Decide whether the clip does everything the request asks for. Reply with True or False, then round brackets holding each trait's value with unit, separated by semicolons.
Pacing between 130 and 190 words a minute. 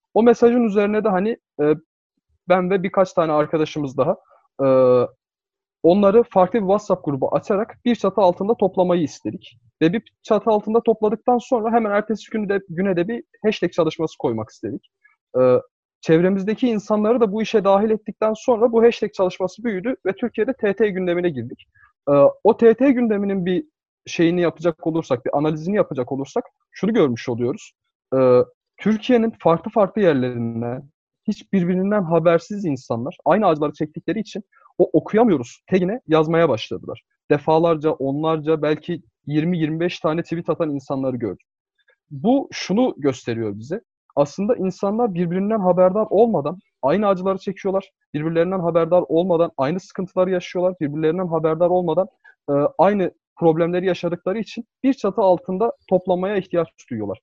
True (135 wpm)